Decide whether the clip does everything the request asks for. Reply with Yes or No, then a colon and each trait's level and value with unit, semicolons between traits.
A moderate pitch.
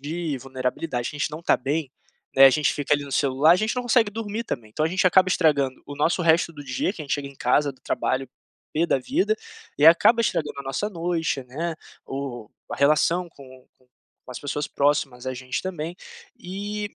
Yes: medium, 150 Hz